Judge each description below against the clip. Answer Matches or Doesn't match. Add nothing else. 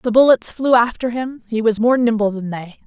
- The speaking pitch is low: Doesn't match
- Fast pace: Matches